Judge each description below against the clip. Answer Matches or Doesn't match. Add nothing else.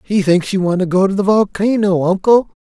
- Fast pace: Matches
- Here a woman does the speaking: Doesn't match